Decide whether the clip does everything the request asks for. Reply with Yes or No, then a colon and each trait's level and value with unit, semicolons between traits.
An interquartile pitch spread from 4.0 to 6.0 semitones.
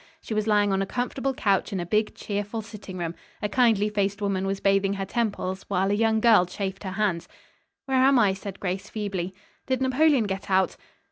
No: narrow, 2.4 semitones